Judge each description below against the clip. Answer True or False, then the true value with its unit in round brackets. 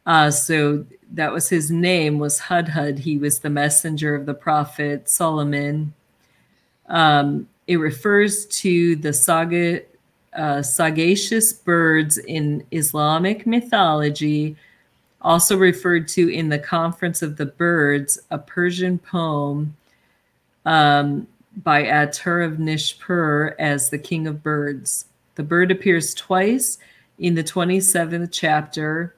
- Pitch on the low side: False (160 Hz)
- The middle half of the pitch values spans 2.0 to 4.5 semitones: True (2.8 semitones)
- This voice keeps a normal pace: False (120 wpm)